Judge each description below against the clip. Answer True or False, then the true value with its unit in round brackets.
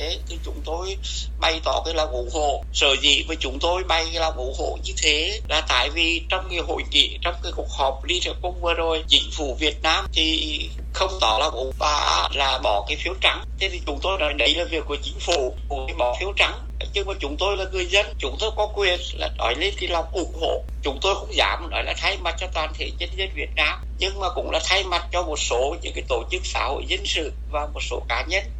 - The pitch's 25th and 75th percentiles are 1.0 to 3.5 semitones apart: False (5.1 semitones)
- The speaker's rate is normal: False (255 wpm)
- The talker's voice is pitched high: False (165 Hz)